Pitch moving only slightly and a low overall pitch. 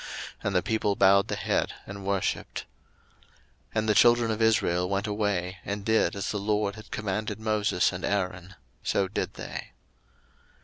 Yes: narrow, 1.9 semitones; low, 100 Hz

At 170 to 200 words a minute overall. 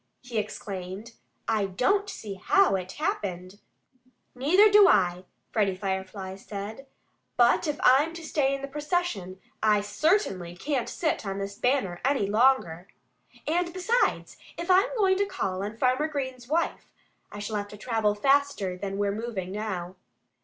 No: average, 155 wpm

